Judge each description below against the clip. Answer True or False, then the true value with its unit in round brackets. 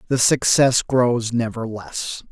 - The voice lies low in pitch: True (120 Hz)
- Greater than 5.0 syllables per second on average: False (3.4 syllables/s)